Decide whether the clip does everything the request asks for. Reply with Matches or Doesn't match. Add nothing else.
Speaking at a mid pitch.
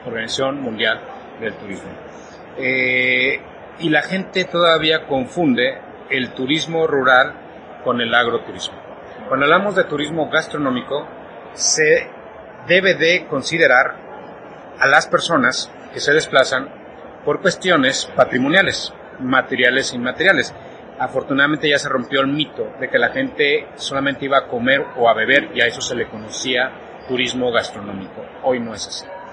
Matches